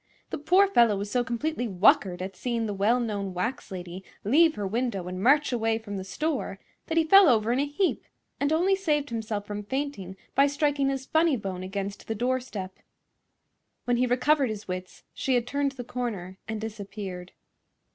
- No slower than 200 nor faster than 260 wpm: No, average, 185 wpm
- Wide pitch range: Yes, wide, 6.0 semitones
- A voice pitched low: No, high, 235 Hz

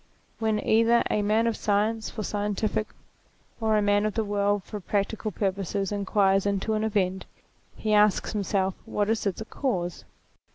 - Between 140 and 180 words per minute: Yes, average, 160 wpm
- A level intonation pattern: Yes, narrow, 1.6 semitones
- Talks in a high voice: Yes, high, 205 Hz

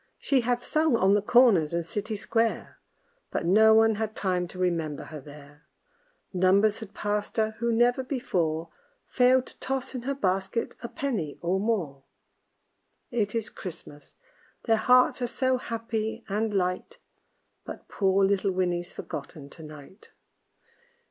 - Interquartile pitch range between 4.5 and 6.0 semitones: Yes, average, 4.8 semitones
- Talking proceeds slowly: No, average, 150 wpm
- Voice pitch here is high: Yes, high, 205 Hz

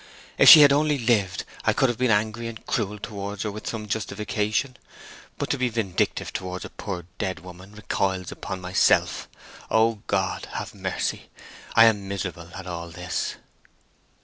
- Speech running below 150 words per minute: No, average, 165 wpm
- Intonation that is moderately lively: Yes, average, 3.3 semitones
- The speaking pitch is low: Yes, low, 105 Hz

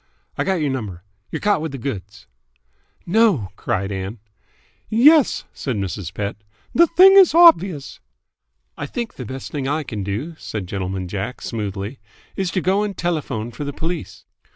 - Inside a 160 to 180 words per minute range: Yes, average, 165 wpm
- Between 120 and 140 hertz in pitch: Yes, low, 135 Hz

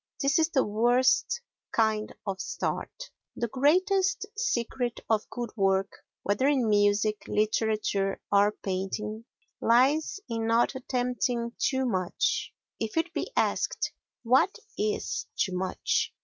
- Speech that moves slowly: Yes, slow, 120 wpm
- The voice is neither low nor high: No, high, 230 Hz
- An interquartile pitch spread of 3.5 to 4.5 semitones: Yes, average, 4.1 semitones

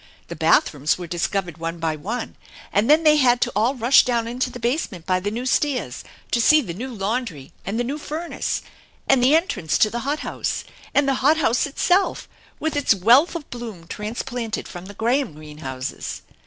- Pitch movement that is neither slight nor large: No, wide, 6.8 semitones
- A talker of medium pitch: No, high, 235 Hz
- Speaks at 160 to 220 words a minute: Yes, average, 195 wpm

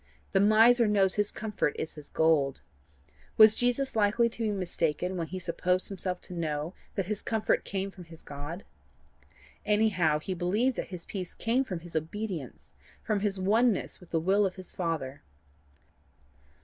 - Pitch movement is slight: No, average, 4.1 semitones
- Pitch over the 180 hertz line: Yes, high, 190 Hz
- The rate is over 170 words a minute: No, average, 165 wpm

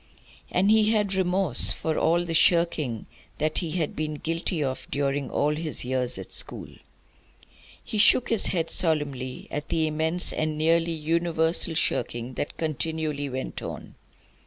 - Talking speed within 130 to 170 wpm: Yes, average, 150 wpm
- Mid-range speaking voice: Yes, medium, 160 Hz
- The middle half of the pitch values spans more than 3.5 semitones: No, average, 2.8 semitones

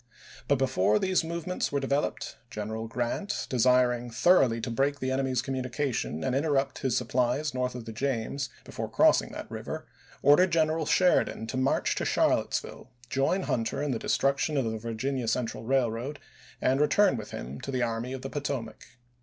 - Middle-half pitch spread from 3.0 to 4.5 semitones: Yes, average, 3.3 semitones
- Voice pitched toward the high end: No, low, 130 Hz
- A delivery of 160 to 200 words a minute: Yes, average, 170 wpm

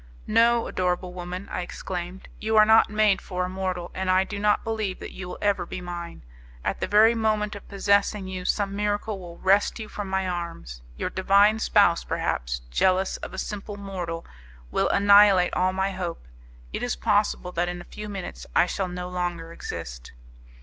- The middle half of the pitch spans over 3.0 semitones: No, narrow, 2.5 semitones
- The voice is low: No, high, 190 Hz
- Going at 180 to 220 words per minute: Yes, average, 190 wpm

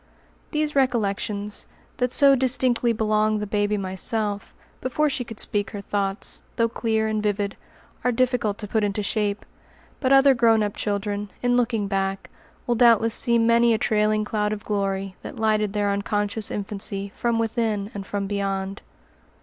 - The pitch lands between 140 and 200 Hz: No, high, 215 Hz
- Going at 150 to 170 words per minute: Yes, average, 160 wpm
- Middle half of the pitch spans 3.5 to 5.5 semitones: No, narrow, 2.5 semitones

